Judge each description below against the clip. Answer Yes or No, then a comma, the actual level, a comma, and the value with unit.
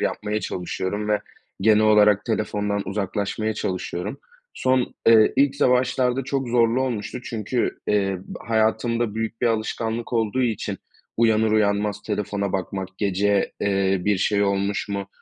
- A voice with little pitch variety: Yes, narrow, 2.3 semitones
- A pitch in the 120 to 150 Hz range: No, low, 105 Hz